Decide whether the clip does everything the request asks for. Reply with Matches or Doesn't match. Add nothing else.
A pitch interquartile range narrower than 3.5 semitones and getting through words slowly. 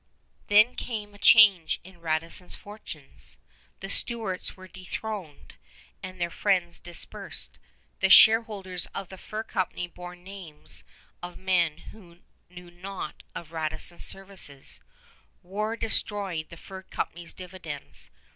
Matches